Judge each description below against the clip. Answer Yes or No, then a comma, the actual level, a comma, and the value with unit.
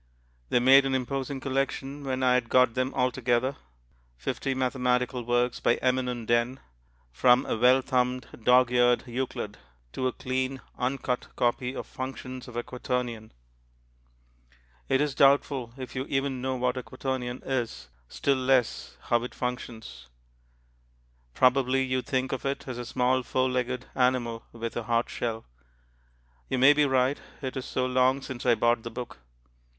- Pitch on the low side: Yes, low, 125 Hz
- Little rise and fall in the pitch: Yes, narrow, 1.3 semitones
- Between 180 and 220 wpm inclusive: No, average, 160 wpm